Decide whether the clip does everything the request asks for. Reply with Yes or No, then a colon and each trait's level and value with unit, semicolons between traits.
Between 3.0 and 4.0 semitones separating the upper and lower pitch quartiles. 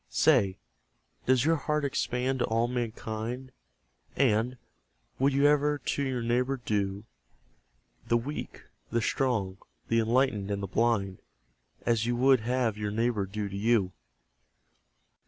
Yes: average, 3.6 semitones